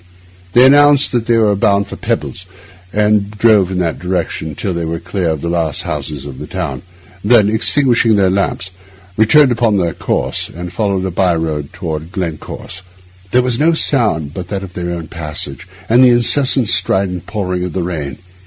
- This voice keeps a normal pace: Yes, average, 185 wpm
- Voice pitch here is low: Yes, very low, 95 Hz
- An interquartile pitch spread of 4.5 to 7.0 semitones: Yes, average, 4.8 semitones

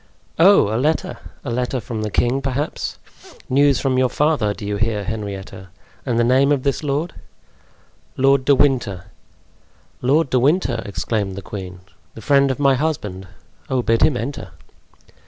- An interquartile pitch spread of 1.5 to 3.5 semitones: No, average, 4.7 semitones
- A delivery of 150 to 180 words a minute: Yes, average, 160 wpm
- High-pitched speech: No, low, 125 Hz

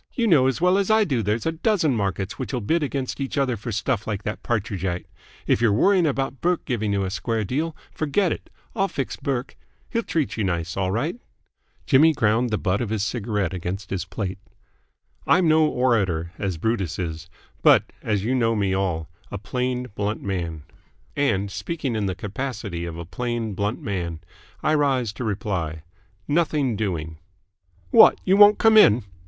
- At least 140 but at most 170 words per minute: No, average, 185 wpm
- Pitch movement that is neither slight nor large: No, wide, 6.3 semitones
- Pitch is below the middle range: Yes, low, 110 Hz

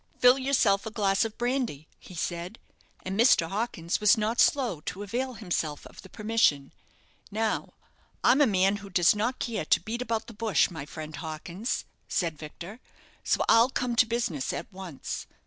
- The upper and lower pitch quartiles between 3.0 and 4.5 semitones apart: No, average, 5.2 semitones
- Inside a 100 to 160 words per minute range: No, average, 175 wpm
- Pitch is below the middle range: No, high, 210 Hz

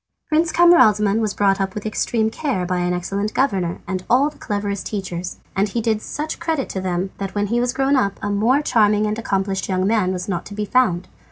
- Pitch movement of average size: Yes, average, 3.9 semitones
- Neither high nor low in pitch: No, high, 205 Hz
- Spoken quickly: Yes, fast, 225 wpm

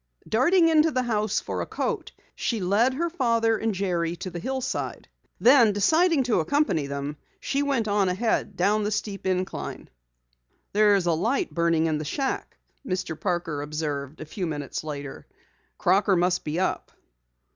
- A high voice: Yes, high, 195 Hz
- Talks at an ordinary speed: Yes, average, 160 wpm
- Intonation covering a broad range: Yes, wide, 6.2 semitones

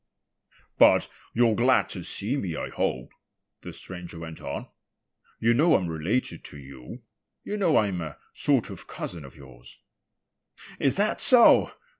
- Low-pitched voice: Yes, very low, 95 Hz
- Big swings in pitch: Yes, wide, 8.3 semitones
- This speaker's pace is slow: No, average, 150 wpm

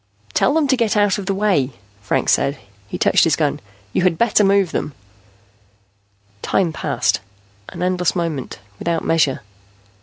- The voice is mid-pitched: Yes, medium, 180 Hz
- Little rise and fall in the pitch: No, average, 4.3 semitones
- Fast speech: No, average, 155 wpm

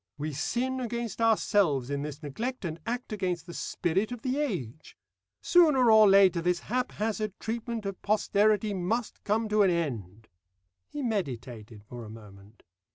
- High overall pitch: Yes, high, 200 Hz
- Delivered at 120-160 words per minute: Yes, average, 155 wpm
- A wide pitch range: Yes, wide, 7.7 semitones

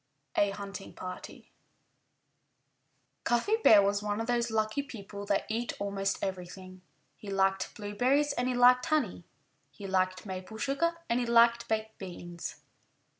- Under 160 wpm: Yes, average, 145 wpm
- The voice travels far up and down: No, average, 3.7 semitones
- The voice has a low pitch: No, high, 210 Hz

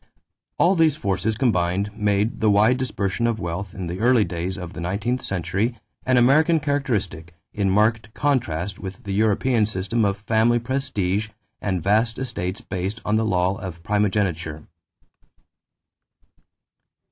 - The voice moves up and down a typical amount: Yes, average, 4.0 semitones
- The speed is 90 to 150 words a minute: Yes, average, 140 wpm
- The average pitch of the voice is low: Yes, low, 105 Hz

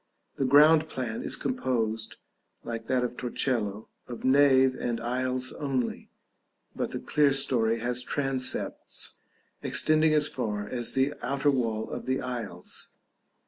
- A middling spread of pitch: Yes, average, 3.0 semitones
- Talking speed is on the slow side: Yes, slow, 130 wpm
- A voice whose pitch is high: No, low, 130 Hz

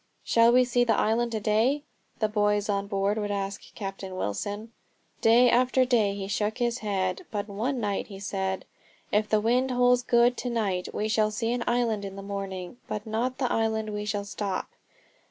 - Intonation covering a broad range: No, average, 3.0 semitones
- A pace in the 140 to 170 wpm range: No, average, 195 wpm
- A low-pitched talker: No, high, 215 Hz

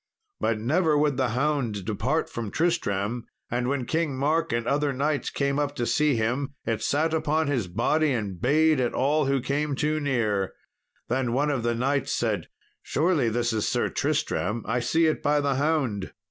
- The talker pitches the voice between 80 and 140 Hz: Yes, low, 135 Hz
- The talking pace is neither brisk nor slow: Yes, average, 185 wpm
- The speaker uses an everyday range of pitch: Yes, average, 4.2 semitones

